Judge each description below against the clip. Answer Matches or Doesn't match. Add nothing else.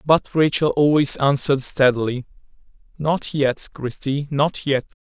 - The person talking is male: Matches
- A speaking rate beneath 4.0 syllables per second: Doesn't match